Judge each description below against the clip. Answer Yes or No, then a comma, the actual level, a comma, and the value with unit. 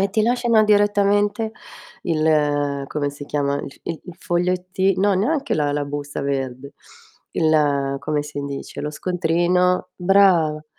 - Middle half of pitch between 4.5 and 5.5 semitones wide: Yes, average, 5.1 semitones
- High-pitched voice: No, medium, 160 Hz